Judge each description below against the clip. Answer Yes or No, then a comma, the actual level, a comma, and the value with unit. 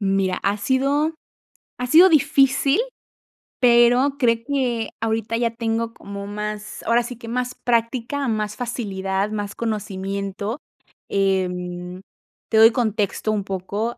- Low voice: No, high, 225 Hz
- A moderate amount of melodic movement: Yes, average, 3.7 semitones